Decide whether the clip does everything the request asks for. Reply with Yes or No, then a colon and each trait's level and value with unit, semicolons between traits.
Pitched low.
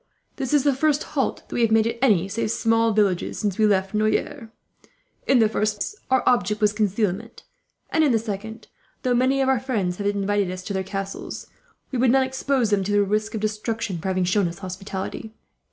No: high, 215 Hz